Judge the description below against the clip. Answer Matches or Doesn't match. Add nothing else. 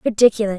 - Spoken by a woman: Matches